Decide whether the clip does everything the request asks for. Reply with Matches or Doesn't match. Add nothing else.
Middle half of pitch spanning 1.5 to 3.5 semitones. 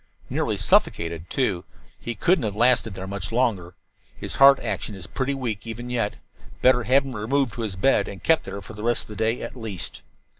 Doesn't match